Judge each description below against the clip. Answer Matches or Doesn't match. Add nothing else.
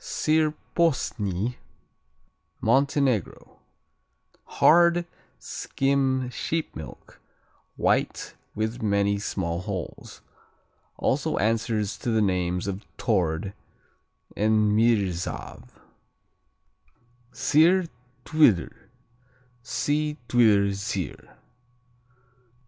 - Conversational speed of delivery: Doesn't match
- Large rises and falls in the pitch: Matches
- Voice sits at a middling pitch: Doesn't match